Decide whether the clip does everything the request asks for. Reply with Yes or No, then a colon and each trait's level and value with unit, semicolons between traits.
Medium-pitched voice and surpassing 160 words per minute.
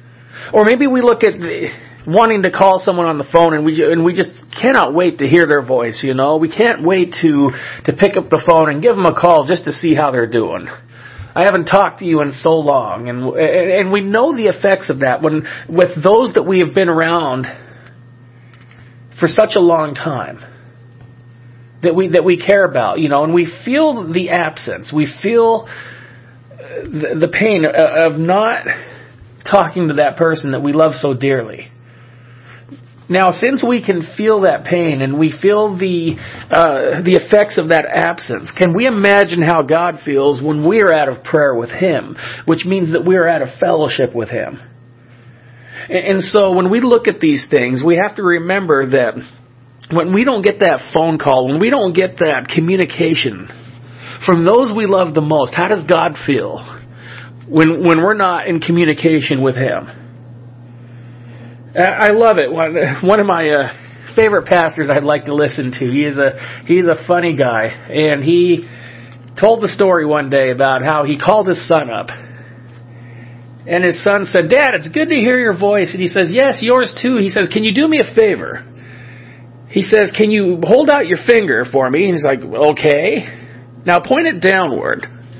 Yes: medium, 160 Hz; average, 185 wpm